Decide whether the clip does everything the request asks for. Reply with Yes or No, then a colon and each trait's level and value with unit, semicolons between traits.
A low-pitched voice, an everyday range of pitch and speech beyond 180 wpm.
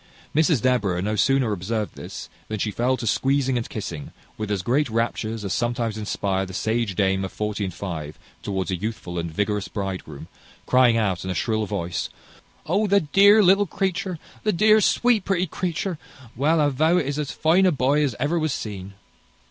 No: low, 115 Hz; wide, 7.7 semitones; average, 190 wpm